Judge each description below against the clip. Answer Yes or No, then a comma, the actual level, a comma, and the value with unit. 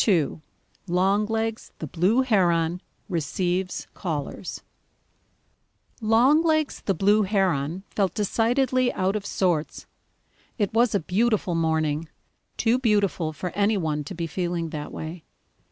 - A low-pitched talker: No, high, 190 Hz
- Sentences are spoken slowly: Yes, slow, 120 wpm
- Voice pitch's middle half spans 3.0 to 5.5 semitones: Yes, average, 4.7 semitones